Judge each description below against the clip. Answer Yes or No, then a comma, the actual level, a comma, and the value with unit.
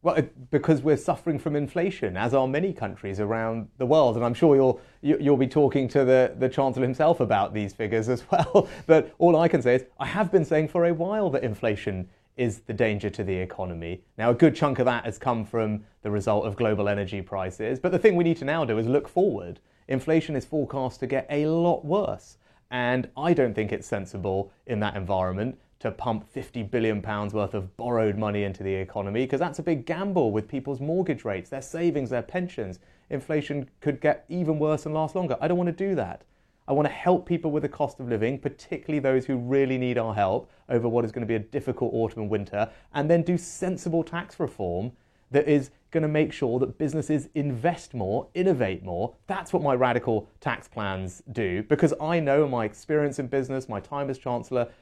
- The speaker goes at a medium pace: No, fast, 215 wpm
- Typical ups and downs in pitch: No, wide, 5.9 semitones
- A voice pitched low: Yes, low, 130 Hz